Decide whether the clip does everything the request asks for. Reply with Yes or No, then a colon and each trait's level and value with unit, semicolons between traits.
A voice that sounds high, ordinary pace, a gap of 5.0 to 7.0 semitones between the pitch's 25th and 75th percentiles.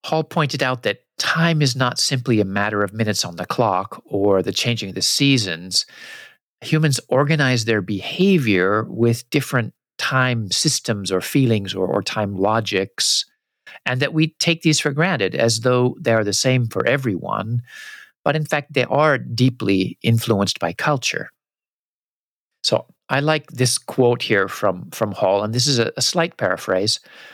No: low, 125 Hz; average, 165 wpm; average, 5.3 semitones